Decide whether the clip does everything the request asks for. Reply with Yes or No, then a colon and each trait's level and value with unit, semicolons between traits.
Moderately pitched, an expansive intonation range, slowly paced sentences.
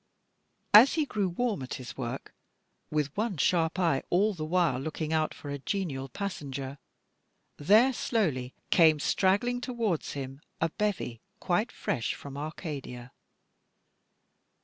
Yes: medium, 160 Hz; wide, 6.6 semitones; slow, 130 wpm